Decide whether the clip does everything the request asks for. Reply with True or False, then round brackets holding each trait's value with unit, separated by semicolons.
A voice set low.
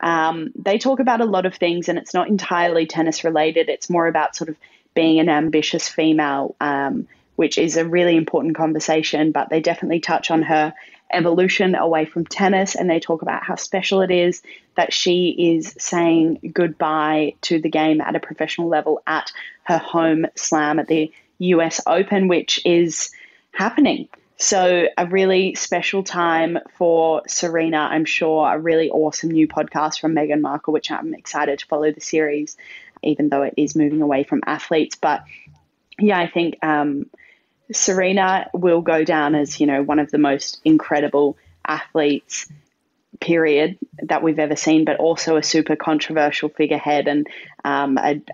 False (160 Hz)